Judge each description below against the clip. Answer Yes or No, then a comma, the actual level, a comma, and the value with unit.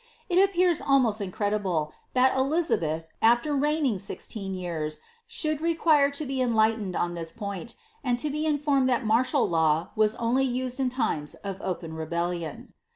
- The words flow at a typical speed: Yes, average, 160 wpm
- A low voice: No, high, 235 Hz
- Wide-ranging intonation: Yes, wide, 7.6 semitones